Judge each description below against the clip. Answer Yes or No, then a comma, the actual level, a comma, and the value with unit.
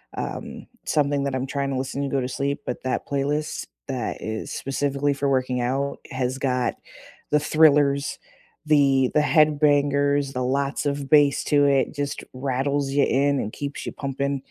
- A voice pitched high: No, medium, 140 Hz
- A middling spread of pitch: No, narrow, 1.2 semitones